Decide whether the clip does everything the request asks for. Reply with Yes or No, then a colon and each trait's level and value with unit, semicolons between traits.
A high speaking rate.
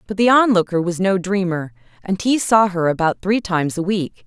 Yes: fast, 210 wpm